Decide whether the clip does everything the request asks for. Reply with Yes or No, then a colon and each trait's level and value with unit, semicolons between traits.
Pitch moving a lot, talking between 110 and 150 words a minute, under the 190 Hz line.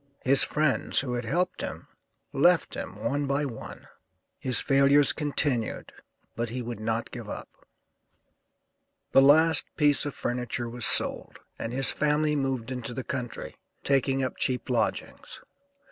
No: average, 3.0 semitones; average, 145 wpm; low, 135 Hz